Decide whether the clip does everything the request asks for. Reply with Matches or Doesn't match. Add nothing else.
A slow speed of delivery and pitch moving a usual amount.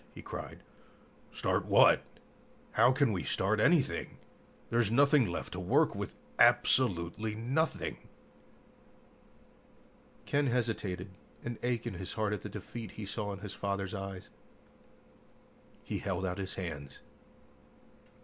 Matches